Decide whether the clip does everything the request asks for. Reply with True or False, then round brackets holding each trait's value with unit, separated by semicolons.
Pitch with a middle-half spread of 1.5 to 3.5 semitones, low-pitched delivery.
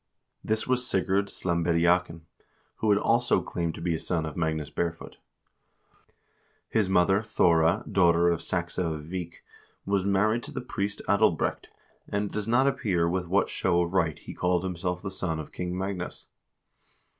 True (2.9 semitones; 90 Hz)